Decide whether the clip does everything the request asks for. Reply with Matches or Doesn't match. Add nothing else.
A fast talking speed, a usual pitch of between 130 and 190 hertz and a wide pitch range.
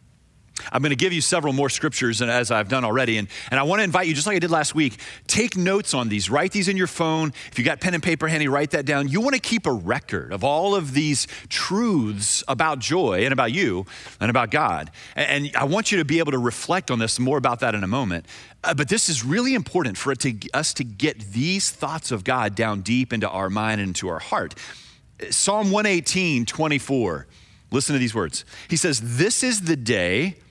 Matches